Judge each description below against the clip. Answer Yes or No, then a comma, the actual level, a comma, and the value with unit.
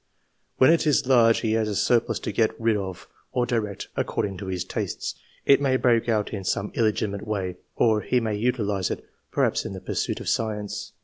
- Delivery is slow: No, average, 200 wpm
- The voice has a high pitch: No, low, 110 Hz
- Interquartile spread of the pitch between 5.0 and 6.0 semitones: No, average, 2.9 semitones